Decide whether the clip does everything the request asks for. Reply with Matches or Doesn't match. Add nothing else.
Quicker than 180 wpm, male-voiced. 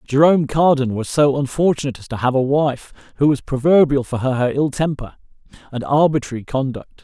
Doesn't match